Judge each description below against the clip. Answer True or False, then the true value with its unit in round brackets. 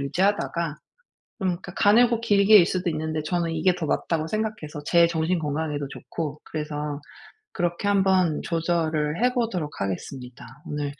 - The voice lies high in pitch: False (165 Hz)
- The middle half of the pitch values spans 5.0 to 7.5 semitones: False (4.0 semitones)